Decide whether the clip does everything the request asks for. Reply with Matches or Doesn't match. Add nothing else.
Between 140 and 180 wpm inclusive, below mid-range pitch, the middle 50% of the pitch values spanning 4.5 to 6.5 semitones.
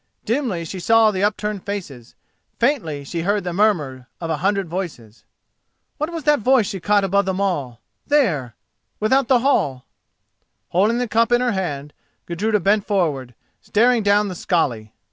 Doesn't match